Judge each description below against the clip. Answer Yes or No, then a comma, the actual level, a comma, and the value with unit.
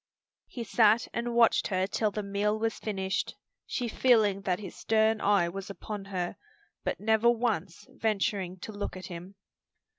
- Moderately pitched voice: No, high, 205 Hz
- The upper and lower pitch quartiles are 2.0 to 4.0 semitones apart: Yes, narrow, 2.4 semitones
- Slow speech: No, average, 160 wpm